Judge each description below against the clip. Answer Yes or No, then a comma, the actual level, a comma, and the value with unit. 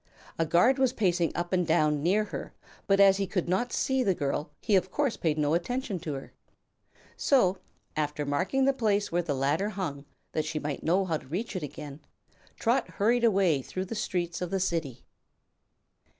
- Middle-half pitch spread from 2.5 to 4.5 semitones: No, average, 4.9 semitones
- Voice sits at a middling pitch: Yes, medium, 180 Hz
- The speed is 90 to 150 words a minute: No, average, 195 wpm